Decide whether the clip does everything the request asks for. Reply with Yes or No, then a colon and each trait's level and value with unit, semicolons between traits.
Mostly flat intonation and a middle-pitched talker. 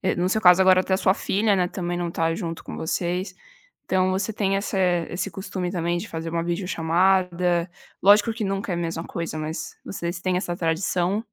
Yes: narrow, 2.1 semitones; medium, 180 Hz